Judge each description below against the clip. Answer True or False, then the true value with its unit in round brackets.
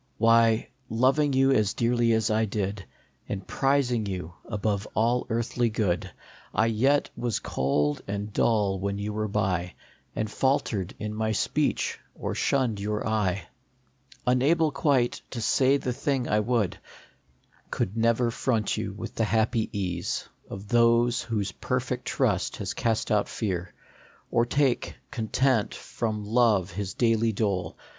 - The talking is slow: False (145 wpm)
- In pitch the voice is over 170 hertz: False (110 Hz)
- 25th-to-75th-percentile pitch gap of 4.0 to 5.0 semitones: False (2.9 semitones)